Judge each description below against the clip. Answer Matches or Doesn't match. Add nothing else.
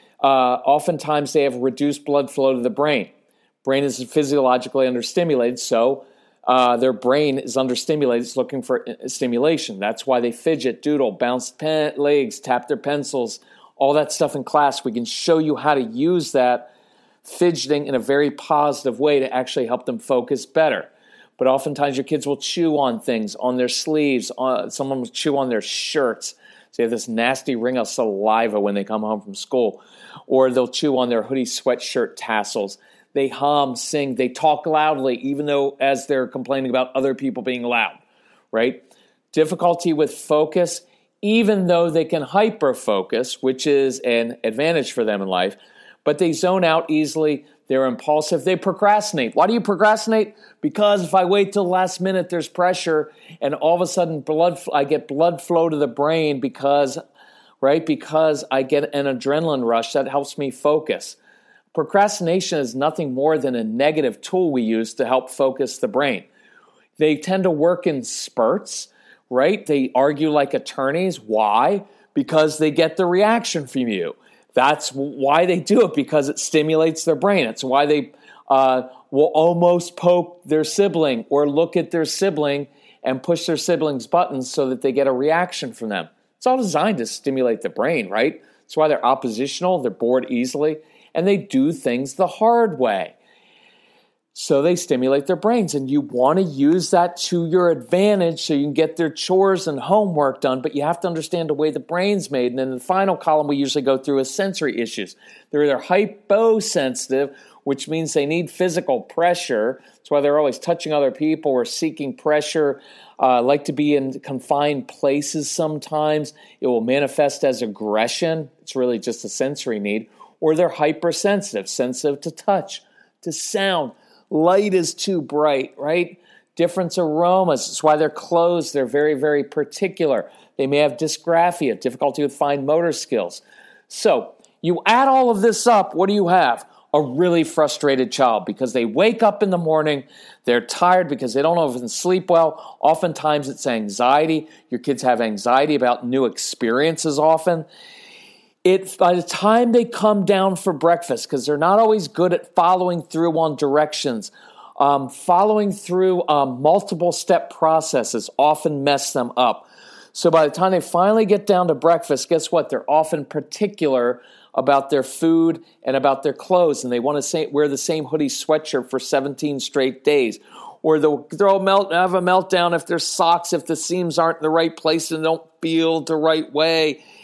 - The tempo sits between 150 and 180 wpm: Matches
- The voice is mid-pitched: Matches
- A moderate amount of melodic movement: Matches